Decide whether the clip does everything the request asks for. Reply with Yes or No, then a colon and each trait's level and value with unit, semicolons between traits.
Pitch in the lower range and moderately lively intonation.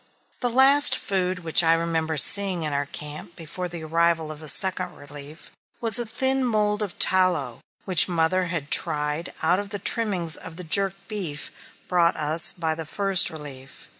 No: medium, 170 Hz; average, 3.8 semitones